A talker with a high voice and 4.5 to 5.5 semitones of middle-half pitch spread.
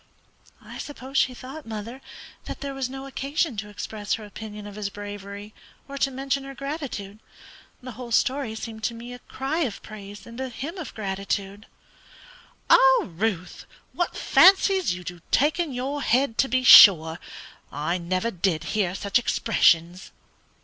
Yes: high, 230 Hz; average, 5.1 semitones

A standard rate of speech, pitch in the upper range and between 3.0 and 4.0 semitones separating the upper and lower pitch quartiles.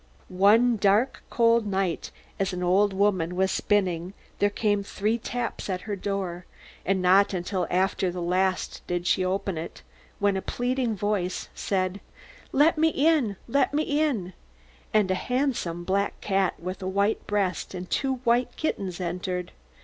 Yes: average, 155 wpm; high, 195 Hz; average, 3.3 semitones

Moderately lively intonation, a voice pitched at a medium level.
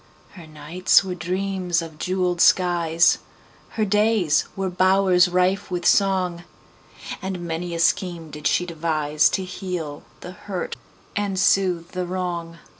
No: narrow, 2.0 semitones; medium, 180 Hz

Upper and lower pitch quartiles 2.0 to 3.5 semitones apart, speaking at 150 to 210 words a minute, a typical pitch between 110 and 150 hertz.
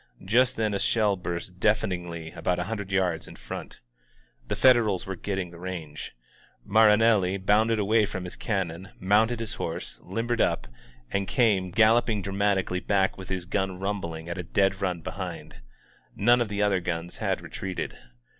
No: average, 3.0 semitones; average, 180 wpm; very low, 95 Hz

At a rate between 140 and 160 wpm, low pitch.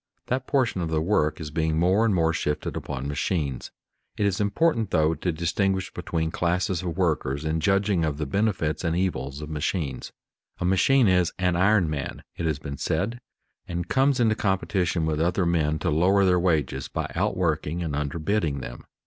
No: average, 185 wpm; very low, 85 Hz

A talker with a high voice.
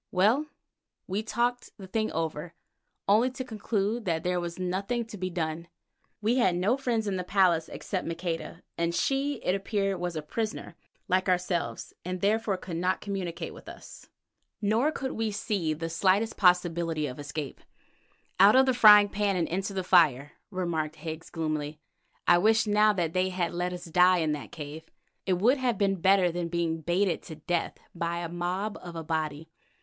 No: medium, 180 Hz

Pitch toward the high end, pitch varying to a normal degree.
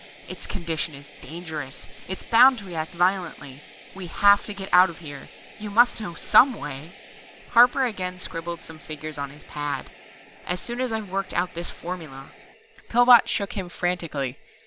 No: medium, 175 Hz; average, 4.5 semitones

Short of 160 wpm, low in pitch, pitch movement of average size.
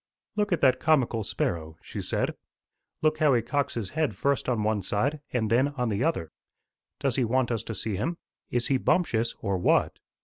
No: average, 200 wpm; low, 120 Hz; average, 4.6 semitones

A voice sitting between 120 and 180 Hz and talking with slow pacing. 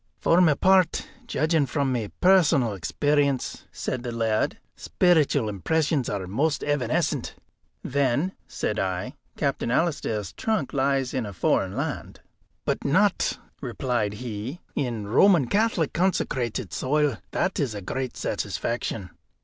Yes: low, 135 Hz; slow, 125 wpm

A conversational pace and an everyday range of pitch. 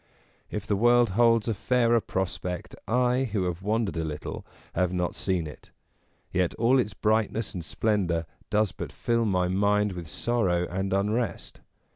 Yes: average, 160 wpm; average, 4.1 semitones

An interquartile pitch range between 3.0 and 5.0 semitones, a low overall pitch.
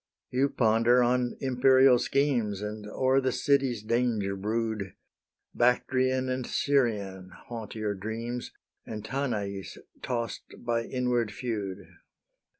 Yes: average, 3.3 semitones; low, 120 Hz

